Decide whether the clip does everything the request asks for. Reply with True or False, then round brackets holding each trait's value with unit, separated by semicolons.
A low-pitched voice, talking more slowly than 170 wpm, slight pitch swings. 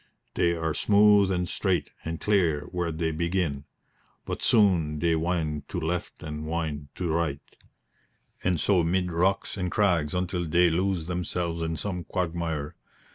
True (85 Hz; 150 wpm; 2.1 semitones)